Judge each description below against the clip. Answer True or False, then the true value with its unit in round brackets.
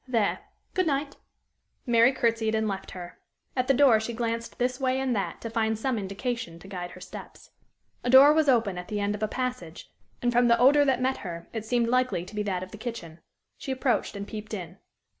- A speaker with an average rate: False (220 wpm)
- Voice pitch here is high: True (230 Hz)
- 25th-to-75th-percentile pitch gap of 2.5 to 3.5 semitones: False (3.9 semitones)